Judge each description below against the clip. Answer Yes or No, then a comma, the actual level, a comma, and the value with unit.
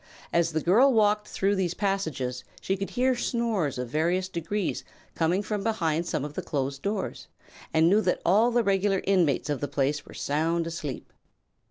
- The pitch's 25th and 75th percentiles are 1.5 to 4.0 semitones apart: No, average, 5.0 semitones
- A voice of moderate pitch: Yes, medium, 180 Hz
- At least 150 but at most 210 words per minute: Yes, average, 180 wpm